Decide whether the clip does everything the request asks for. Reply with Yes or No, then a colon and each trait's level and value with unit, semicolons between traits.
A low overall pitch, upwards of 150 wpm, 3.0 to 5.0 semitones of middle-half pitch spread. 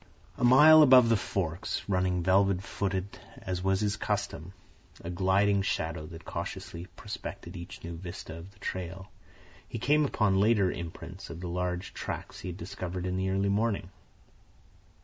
No: very low, 95 Hz; average, 160 wpm; narrow, 2.4 semitones